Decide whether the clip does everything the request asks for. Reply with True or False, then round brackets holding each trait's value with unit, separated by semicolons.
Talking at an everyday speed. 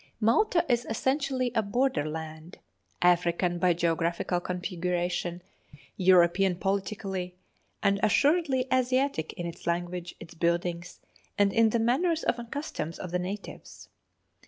False (120 wpm)